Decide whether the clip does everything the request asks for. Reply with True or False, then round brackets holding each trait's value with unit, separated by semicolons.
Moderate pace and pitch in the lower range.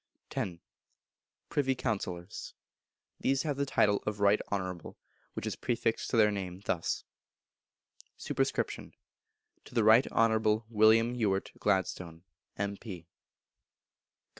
False (110 wpm; 105 Hz)